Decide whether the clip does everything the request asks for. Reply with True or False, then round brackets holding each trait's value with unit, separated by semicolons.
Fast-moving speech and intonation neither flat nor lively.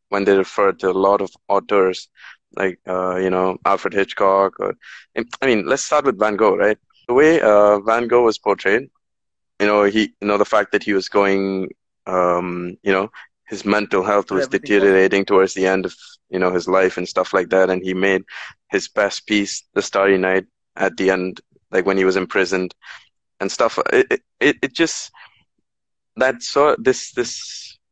False (195 wpm; 1.7 semitones)